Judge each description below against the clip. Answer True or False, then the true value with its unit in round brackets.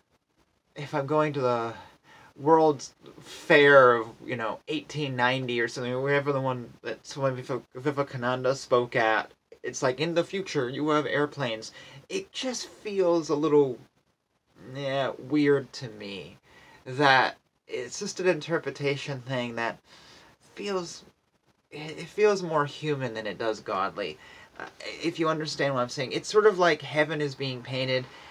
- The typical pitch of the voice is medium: True (145 Hz)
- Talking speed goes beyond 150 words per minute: False (145 wpm)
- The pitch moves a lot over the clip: False (3.8 semitones)